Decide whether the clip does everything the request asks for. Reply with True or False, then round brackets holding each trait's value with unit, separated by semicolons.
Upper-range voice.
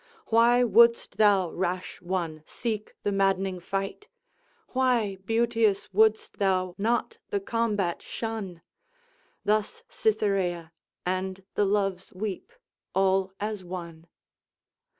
True (195 Hz)